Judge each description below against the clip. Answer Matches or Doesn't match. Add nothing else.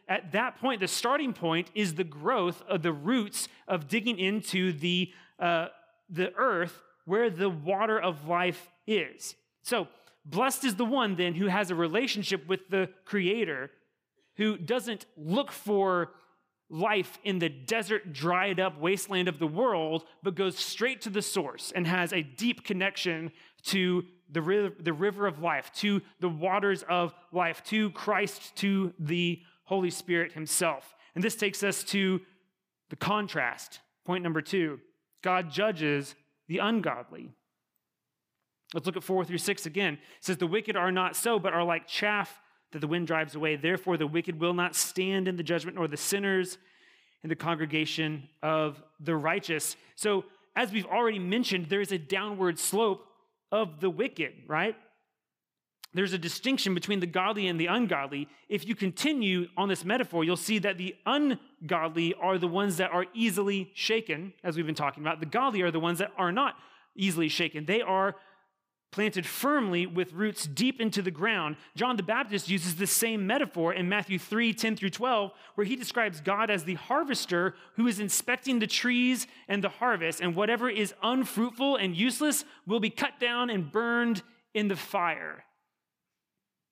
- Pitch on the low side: Doesn't match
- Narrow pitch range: Doesn't match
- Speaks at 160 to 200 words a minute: Matches